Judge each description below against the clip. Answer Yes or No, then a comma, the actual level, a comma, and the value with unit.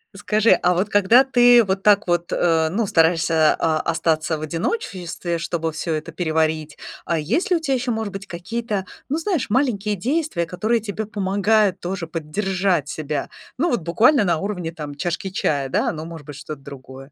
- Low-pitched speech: No, medium, 180 Hz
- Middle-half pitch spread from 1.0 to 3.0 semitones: No, average, 4.9 semitones